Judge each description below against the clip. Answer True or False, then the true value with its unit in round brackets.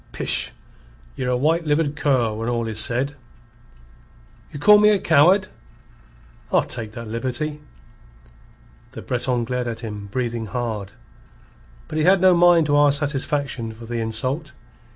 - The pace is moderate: True (150 wpm)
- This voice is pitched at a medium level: False (130 Hz)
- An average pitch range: True (4.6 semitones)